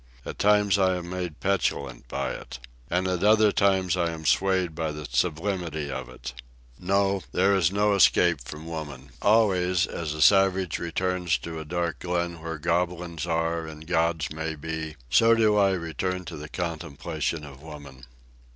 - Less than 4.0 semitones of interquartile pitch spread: Yes, average, 3.0 semitones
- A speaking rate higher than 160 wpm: Yes, average, 170 wpm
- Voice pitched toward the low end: Yes, very low, 85 Hz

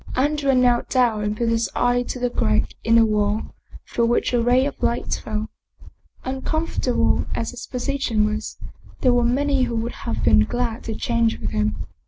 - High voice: Yes, high, 240 Hz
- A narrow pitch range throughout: Yes, narrow, 2.2 semitones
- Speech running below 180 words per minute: No, average, 185 wpm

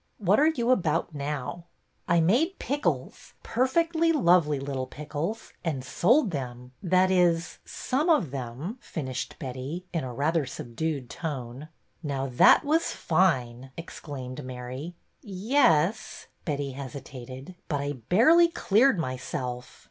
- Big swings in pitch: Yes, wide, 7.0 semitones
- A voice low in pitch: No, medium, 155 Hz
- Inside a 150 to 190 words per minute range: No, average, 140 wpm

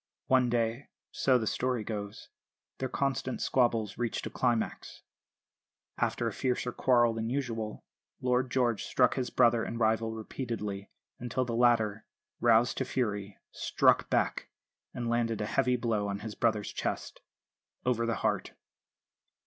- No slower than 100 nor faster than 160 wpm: Yes, average, 140 wpm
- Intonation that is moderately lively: No, narrow, 2.1 semitones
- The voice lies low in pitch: Yes, low, 115 Hz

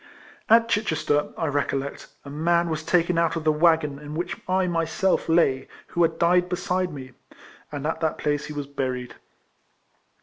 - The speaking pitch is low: No, medium, 160 Hz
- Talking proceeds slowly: No, average, 175 wpm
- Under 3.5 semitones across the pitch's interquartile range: Yes, average, 2.9 semitones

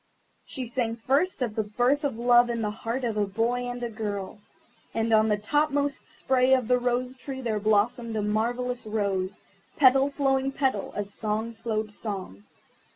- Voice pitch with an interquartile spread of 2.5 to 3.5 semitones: Yes, average, 3.1 semitones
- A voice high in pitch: Yes, high, 235 Hz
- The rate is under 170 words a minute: No, average, 180 wpm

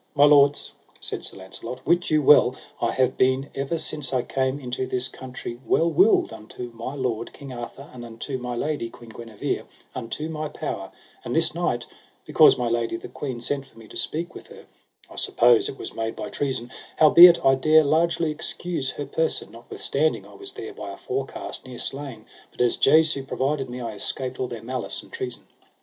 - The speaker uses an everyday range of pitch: Yes, average, 4.1 semitones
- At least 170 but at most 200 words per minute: Yes, average, 195 wpm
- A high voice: No, low, 130 Hz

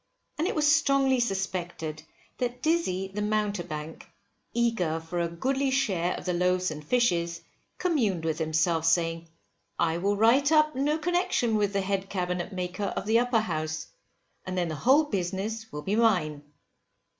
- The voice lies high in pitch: Yes, high, 195 Hz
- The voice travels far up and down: Yes, wide, 6.1 semitones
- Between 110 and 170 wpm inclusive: Yes, average, 160 wpm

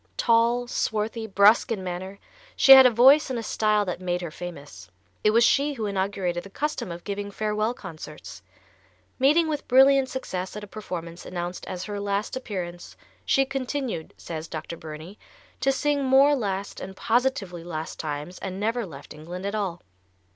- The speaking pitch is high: Yes, high, 205 Hz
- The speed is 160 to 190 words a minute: Yes, average, 170 wpm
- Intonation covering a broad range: Yes, wide, 5.7 semitones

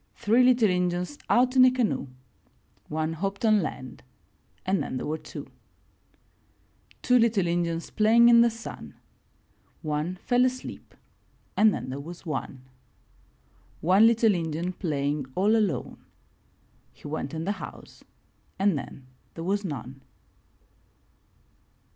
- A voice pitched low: No, medium, 185 Hz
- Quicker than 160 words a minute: No, slow, 135 wpm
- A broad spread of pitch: Yes, wide, 6.3 semitones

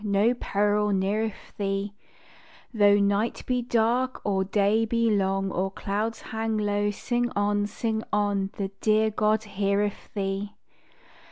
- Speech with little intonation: Yes, narrow, 1.7 semitones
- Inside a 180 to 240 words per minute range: No, slow, 135 wpm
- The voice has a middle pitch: No, high, 205 Hz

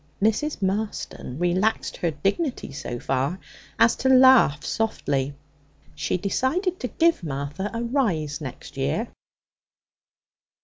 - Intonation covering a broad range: Yes, wide, 9.0 semitones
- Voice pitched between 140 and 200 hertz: Yes, high, 190 Hz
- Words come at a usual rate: No, slow, 115 wpm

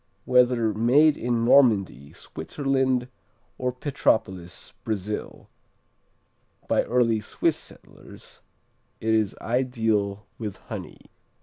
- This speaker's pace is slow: Yes, slow, 90 wpm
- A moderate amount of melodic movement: Yes, average, 3.2 semitones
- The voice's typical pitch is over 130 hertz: No, low, 115 Hz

